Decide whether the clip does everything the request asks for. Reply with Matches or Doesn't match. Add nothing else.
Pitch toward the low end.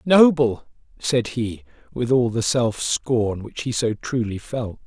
Matches